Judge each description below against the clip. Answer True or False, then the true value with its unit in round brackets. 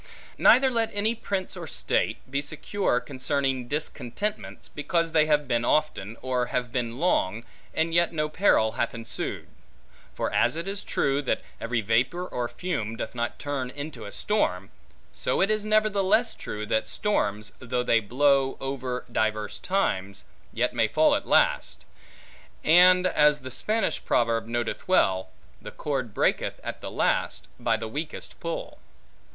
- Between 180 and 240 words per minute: False (155 wpm)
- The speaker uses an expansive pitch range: True (6.8 semitones)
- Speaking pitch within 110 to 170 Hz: True (135 Hz)